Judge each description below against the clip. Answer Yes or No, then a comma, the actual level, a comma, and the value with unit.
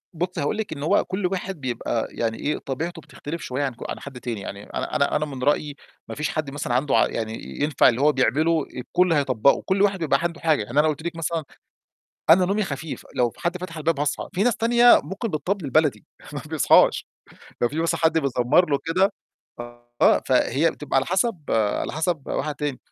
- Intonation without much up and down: No, average, 4.3 semitones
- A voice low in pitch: No, medium, 150 Hz